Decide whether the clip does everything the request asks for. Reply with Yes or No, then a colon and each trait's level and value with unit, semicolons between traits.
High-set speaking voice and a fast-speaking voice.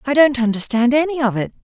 Yes: very high, 255 Hz; fast, 220 wpm